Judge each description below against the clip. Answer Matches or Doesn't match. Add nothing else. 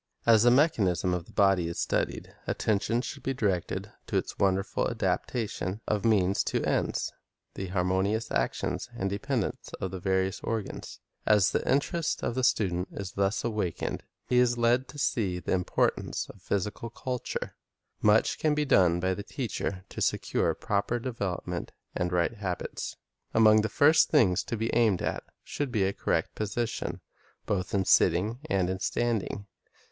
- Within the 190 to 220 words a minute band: Doesn't match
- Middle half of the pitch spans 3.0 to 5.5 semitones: Matches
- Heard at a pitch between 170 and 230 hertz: Doesn't match